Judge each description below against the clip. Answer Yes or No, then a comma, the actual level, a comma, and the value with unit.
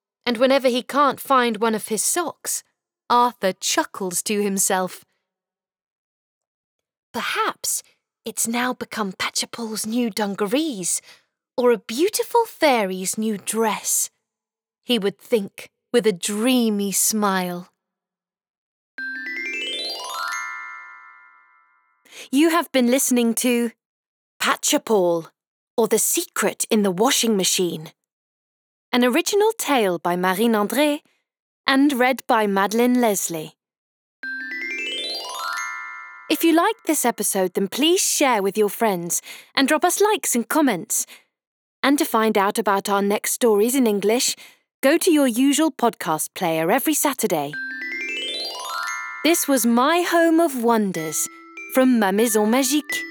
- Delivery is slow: Yes, slow, 115 wpm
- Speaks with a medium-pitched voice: No, high, 225 Hz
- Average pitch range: No, wide, 6.3 semitones